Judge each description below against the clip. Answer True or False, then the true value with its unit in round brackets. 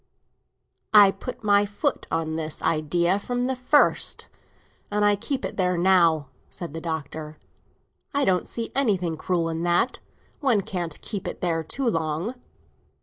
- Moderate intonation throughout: True (4.3 semitones)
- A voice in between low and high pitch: True (180 Hz)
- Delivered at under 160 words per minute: True (150 wpm)